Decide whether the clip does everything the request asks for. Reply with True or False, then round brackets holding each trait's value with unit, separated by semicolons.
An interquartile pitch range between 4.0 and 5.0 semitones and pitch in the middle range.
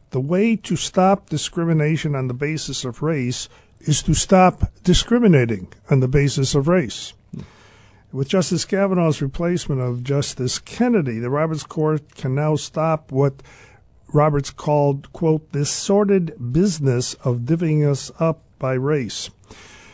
True (4.4 semitones; 145 Hz)